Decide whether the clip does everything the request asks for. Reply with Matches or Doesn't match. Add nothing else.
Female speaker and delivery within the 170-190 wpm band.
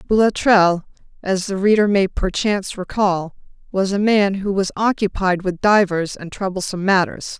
Doesn't match